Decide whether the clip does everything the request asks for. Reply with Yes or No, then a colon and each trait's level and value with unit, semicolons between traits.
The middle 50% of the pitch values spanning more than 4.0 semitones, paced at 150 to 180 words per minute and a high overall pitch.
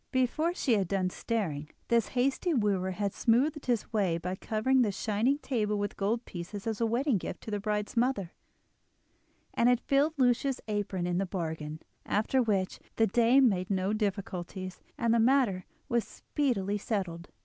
Yes: average, 4.5 semitones; average, 170 wpm; high, 210 Hz